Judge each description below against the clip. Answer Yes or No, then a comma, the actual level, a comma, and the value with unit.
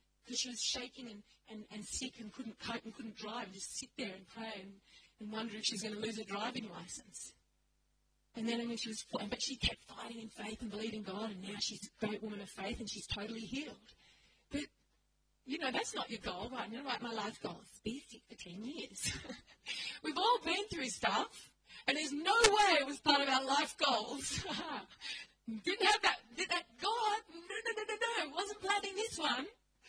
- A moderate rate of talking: No, fast, 215 wpm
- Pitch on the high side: Yes, high, 235 Hz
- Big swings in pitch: Yes, wide, 5.8 semitones